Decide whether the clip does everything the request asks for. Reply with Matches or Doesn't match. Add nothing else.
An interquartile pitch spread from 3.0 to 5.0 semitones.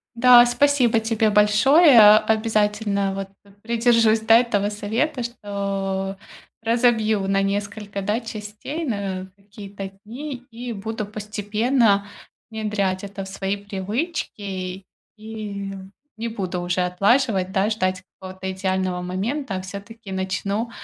Doesn't match